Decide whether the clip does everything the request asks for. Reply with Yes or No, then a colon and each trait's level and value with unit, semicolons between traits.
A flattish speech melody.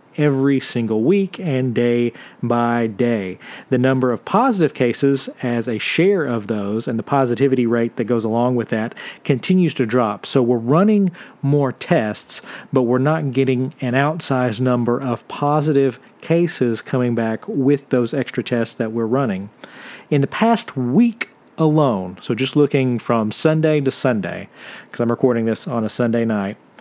No: average, 3.3 semitones